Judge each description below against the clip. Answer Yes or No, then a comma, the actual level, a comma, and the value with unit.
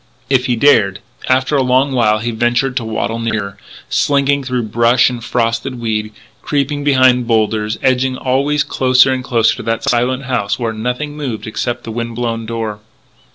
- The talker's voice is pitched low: Yes, low, 120 Hz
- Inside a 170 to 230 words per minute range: Yes, average, 175 wpm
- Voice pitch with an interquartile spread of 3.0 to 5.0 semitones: No, narrow, 2.5 semitones